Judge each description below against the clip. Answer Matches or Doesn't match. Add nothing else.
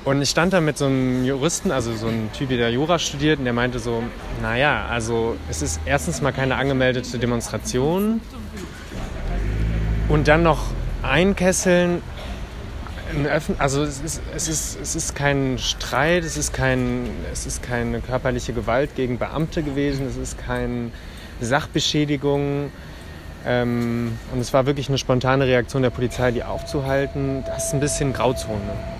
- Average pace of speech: Matches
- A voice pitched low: Matches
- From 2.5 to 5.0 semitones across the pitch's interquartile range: Matches